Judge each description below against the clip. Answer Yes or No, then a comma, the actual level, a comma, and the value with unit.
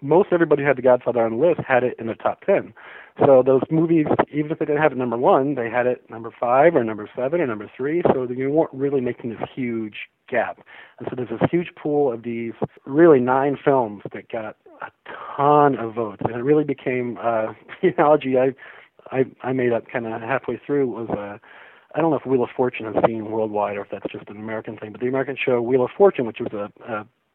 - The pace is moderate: No, fast, 240 wpm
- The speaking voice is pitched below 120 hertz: No, low, 130 Hz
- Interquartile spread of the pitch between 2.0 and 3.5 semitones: No, average, 3.9 semitones